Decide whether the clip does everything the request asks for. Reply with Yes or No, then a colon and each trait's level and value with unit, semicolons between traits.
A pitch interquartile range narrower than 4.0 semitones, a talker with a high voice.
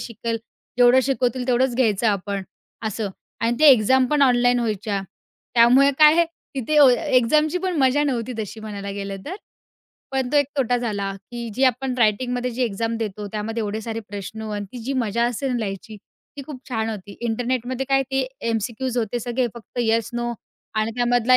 Yes: average, 3.0 semitones; high, 240 Hz